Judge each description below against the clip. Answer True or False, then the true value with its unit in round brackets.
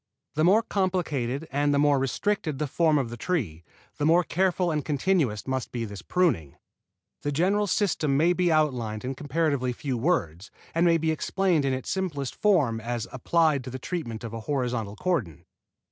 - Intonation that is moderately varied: False (5.8 semitones)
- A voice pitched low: False (145 Hz)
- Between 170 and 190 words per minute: True (180 wpm)